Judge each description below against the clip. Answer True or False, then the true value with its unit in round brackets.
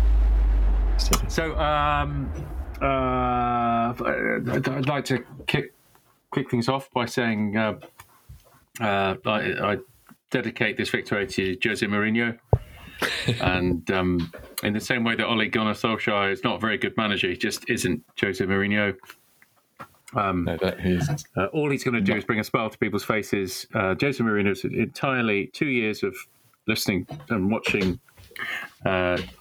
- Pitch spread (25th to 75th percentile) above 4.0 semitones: True (5.2 semitones)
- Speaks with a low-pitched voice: True (110 Hz)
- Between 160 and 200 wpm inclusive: False (140 wpm)